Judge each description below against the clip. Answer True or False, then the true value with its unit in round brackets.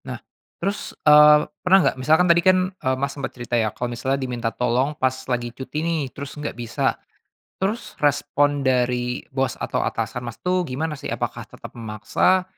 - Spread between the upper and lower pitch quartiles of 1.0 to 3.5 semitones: False (3.9 semitones)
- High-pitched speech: False (135 Hz)